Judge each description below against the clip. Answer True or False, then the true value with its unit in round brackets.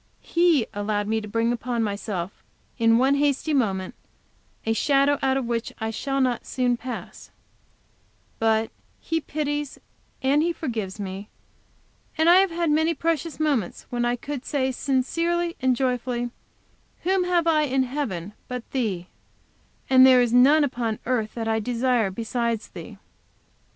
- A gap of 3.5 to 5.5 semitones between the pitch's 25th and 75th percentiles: True (4.6 semitones)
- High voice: True (250 Hz)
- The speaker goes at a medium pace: True (150 wpm)